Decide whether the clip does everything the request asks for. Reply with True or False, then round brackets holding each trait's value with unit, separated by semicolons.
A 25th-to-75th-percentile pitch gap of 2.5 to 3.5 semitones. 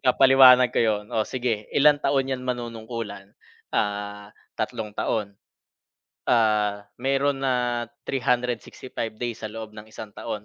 True (3.1 semitones)